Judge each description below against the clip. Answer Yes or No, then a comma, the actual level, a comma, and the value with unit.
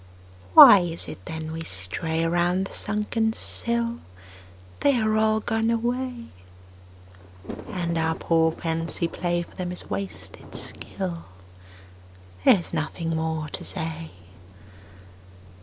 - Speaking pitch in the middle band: Yes, medium, 175 Hz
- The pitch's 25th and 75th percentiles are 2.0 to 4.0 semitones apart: No, average, 5.1 semitones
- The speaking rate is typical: No, slow, 120 wpm